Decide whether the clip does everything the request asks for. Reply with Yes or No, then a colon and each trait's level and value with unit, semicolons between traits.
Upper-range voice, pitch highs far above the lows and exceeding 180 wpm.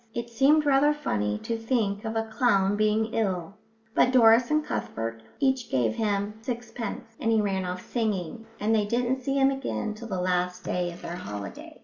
No: high, 220 Hz; average, 4.7 semitones; average, 190 wpm